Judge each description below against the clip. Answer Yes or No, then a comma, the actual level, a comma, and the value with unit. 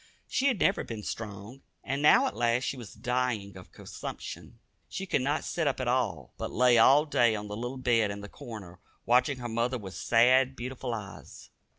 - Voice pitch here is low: Yes, low, 120 Hz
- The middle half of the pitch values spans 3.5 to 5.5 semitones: No, average, 3.1 semitones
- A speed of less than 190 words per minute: No, average, 200 wpm